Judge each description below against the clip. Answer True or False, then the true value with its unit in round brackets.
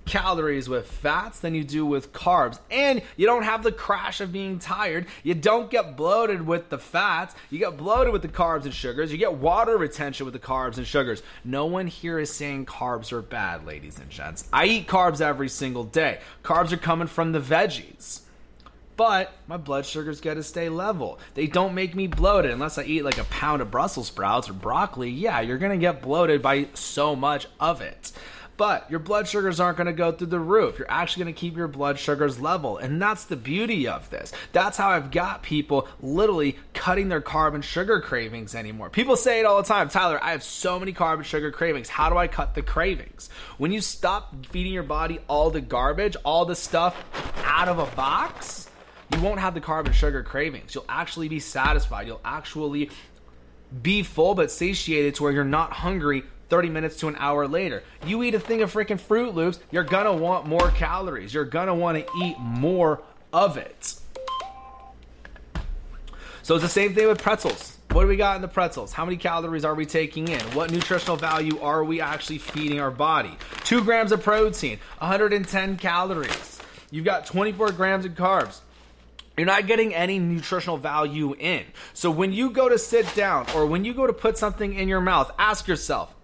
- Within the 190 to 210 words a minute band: True (200 wpm)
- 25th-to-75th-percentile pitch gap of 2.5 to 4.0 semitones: False (4.5 semitones)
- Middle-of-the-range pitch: True (170 Hz)